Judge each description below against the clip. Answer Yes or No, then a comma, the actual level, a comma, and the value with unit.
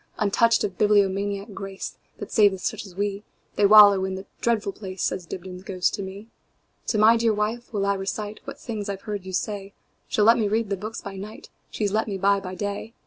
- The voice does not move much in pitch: Yes, narrow, 1.7 semitones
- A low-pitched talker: No, high, 200 Hz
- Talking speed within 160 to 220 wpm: Yes, average, 195 wpm